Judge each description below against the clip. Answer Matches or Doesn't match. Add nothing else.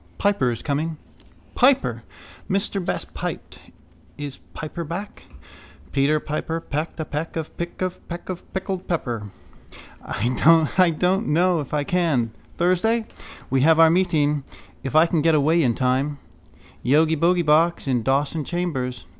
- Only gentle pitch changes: Doesn't match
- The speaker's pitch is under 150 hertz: Doesn't match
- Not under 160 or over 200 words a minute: Doesn't match